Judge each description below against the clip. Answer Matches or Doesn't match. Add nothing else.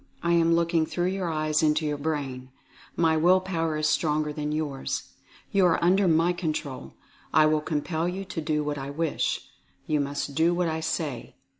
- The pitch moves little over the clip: Matches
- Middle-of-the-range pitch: Matches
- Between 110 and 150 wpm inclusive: Doesn't match